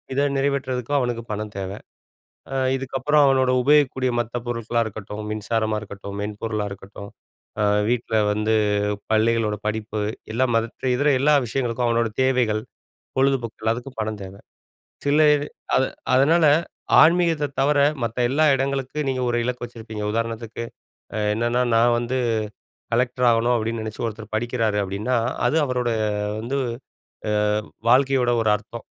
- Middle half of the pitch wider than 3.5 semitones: No, average, 3.2 semitones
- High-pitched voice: No, low, 120 Hz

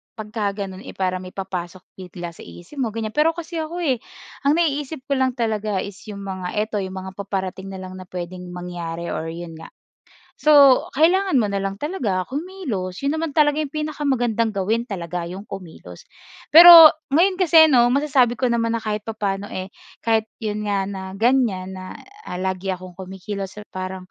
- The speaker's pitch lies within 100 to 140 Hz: No, high, 210 Hz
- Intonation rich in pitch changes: Yes, wide, 6.6 semitones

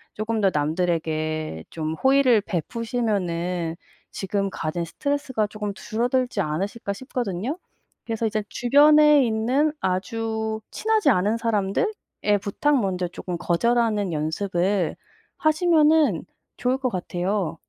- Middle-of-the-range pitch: No, high, 210 Hz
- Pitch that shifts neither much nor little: No, wide, 5.7 semitones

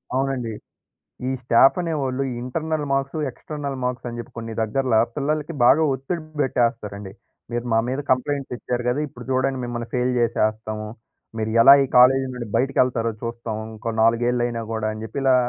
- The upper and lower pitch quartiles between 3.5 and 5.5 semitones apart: No, average, 2.8 semitones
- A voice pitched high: No, low, 125 Hz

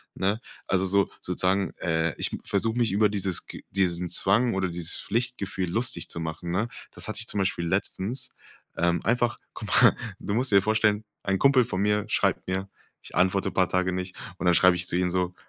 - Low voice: Yes, very low, 95 Hz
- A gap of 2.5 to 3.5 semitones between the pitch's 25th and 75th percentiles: Yes, average, 2.9 semitones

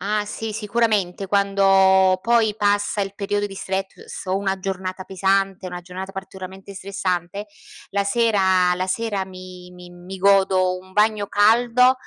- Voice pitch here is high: Yes, high, 195 Hz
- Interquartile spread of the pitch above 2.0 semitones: No, narrow, 1.6 semitones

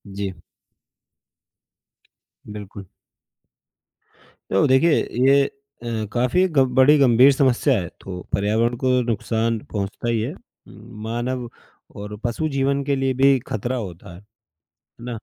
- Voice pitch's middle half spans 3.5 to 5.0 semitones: Yes, average, 4.1 semitones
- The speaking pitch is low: Yes, low, 120 Hz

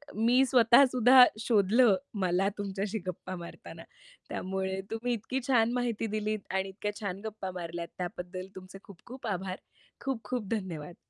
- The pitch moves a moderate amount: Yes, average, 4.2 semitones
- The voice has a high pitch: Yes, high, 205 Hz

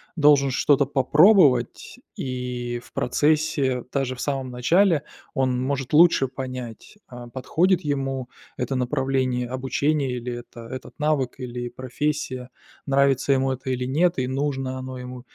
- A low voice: Yes, low, 130 Hz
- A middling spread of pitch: No, narrow, 2.1 semitones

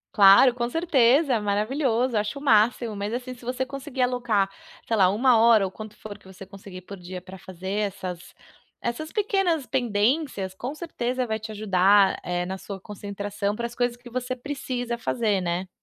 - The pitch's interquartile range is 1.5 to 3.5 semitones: No, average, 4.3 semitones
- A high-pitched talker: Yes, high, 220 Hz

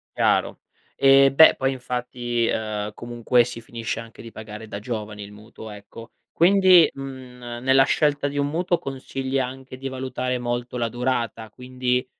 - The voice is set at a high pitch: No, low, 125 Hz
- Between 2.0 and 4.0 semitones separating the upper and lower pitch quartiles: Yes, narrow, 2.6 semitones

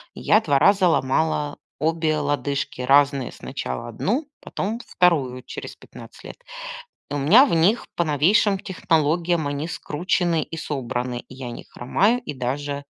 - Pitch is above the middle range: No, medium, 150 Hz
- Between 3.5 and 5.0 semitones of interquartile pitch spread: Yes, average, 4.3 semitones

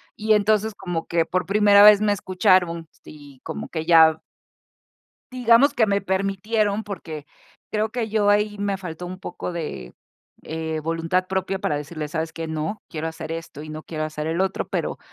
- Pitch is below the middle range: No, medium, 180 Hz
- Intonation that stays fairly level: No, average, 4.3 semitones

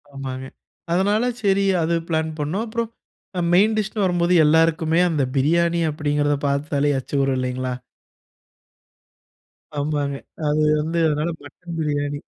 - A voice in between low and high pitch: Yes, medium, 155 Hz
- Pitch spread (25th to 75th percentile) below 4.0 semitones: Yes, average, 3.1 semitones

